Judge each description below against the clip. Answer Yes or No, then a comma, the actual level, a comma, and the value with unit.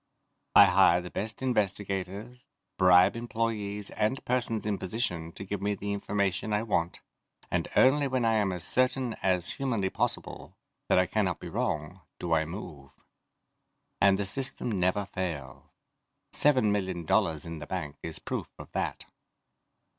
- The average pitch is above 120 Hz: No, low, 100 Hz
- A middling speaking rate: Yes, average, 155 wpm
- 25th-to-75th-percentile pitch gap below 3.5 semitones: No, average, 3.8 semitones